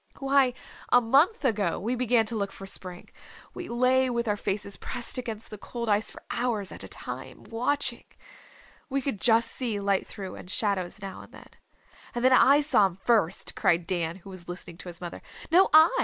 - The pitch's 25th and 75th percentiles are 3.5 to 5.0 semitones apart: Yes, average, 4.6 semitones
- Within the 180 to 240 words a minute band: Yes, average, 200 wpm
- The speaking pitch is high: Yes, high, 225 Hz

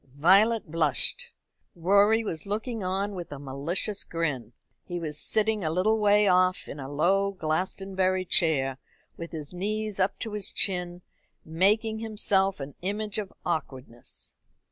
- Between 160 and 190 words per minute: No, average, 145 wpm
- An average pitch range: Yes, average, 4.4 semitones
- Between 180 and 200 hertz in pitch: Yes, medium, 185 Hz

